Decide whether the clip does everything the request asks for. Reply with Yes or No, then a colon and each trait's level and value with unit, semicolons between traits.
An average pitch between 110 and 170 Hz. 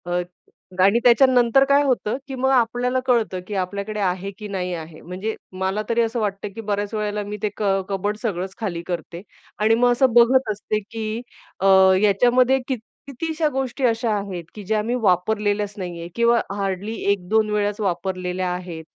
No: high, 210 Hz